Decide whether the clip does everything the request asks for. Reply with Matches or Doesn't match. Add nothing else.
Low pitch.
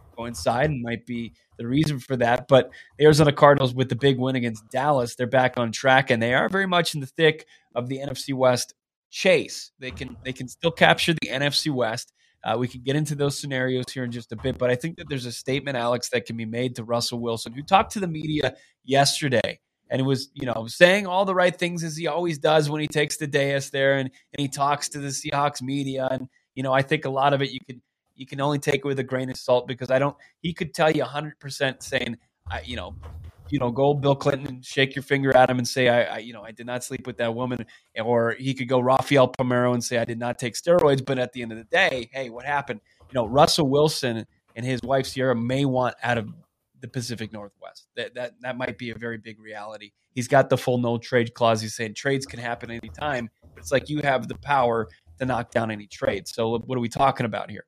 Matches